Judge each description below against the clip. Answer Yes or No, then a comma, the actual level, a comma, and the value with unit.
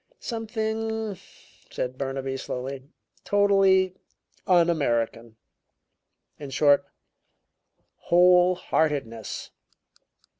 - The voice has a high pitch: No, medium, 170 Hz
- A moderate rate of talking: No, slow, 65 wpm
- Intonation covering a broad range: Yes, wide, 6.7 semitones